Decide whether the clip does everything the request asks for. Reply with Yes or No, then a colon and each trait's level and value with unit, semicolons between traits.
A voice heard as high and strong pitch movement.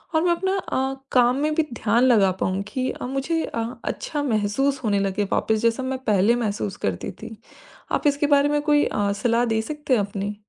Yes: high, 245 Hz; wide, 5.7 semitones